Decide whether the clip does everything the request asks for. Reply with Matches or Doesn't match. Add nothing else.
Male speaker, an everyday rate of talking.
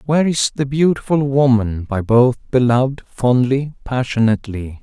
Doesn't match